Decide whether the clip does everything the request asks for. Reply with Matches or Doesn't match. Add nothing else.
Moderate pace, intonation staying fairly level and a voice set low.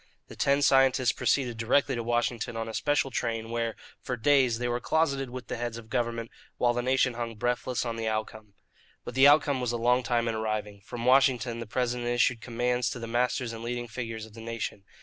Doesn't match